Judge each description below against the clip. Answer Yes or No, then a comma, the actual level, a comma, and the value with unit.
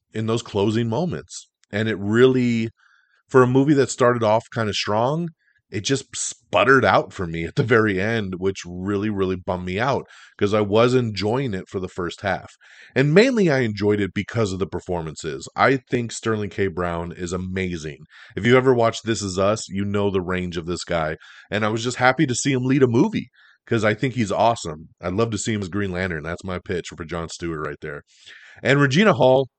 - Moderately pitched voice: No, low, 105 Hz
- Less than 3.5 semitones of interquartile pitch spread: No, average, 4.9 semitones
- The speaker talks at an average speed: No, fast, 215 wpm